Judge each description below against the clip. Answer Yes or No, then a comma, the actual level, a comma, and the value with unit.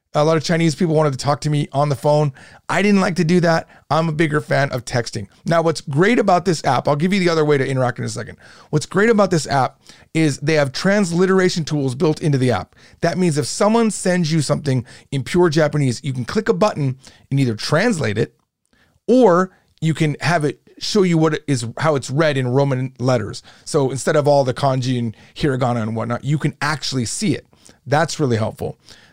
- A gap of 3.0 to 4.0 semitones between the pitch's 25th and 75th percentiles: No, average, 4.6 semitones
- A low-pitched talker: No, medium, 150 Hz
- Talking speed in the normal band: No, fast, 225 wpm